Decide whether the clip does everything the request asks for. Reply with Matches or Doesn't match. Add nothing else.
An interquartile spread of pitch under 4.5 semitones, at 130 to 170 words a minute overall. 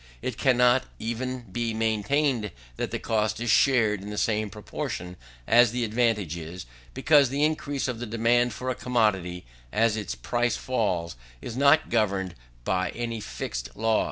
Matches